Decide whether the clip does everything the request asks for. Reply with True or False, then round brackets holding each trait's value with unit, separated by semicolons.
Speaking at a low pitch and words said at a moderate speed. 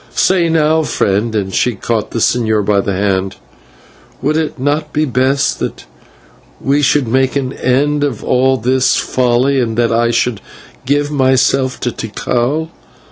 True (130 Hz; 155 wpm)